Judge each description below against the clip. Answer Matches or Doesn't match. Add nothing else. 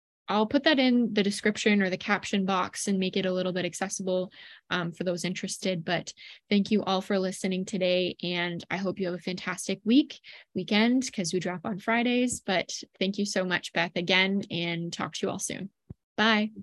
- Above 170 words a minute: Matches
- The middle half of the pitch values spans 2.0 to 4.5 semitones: Matches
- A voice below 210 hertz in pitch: Matches